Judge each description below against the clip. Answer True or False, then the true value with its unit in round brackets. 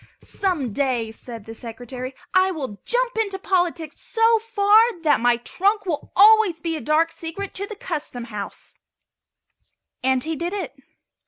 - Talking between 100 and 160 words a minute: True (155 wpm)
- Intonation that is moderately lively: False (7.7 semitones)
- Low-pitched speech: False (330 Hz)